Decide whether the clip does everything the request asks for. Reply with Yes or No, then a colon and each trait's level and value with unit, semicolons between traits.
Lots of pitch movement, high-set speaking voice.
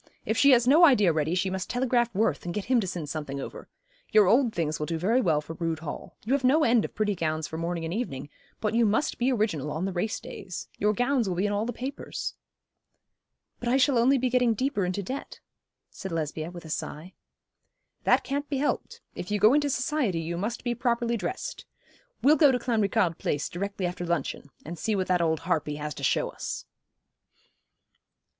Yes: wide, 6.7 semitones; high, 205 Hz